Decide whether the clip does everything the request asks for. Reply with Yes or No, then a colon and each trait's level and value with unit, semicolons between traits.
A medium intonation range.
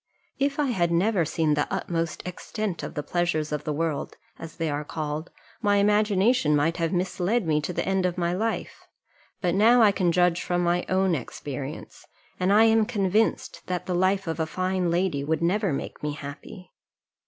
Yes: average, 3.6 semitones